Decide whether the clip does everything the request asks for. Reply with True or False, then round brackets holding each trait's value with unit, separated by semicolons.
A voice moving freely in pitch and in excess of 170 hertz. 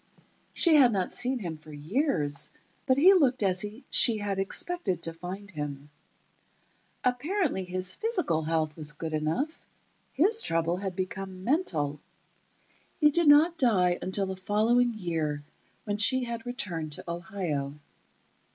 True (7.7 semitones; 190 Hz)